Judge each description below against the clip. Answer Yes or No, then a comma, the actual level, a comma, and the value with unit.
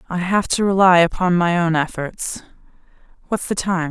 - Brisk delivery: No, average, 170 wpm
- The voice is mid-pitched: Yes, medium, 180 Hz